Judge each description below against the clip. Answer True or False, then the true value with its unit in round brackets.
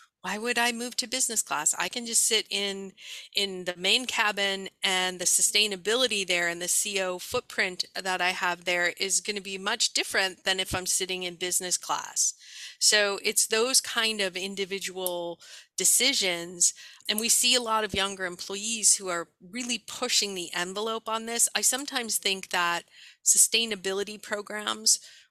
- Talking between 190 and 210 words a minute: False (165 wpm)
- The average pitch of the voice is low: False (195 Hz)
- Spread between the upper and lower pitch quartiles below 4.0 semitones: True (3.4 semitones)